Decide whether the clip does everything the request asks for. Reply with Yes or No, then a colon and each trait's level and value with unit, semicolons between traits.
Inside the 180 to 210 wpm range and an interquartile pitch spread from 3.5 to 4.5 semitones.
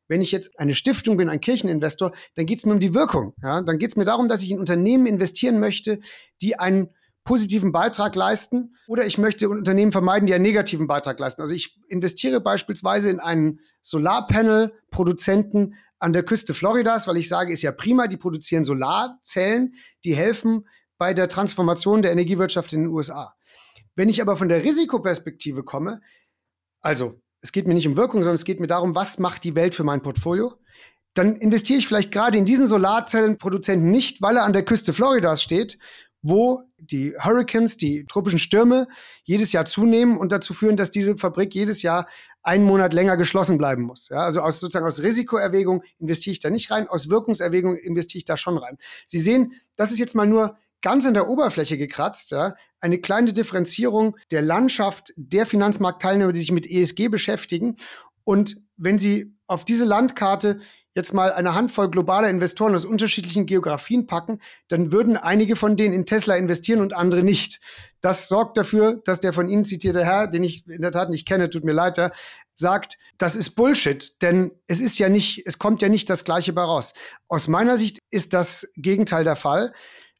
Yes: fast, 190 wpm; average, 3.8 semitones